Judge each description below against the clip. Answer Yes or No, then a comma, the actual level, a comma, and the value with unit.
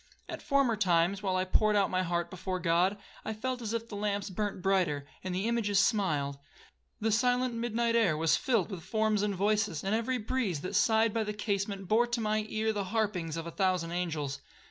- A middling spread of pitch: Yes, average, 3.4 semitones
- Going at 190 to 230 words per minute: Yes, fast, 205 wpm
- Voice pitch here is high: Yes, high, 205 Hz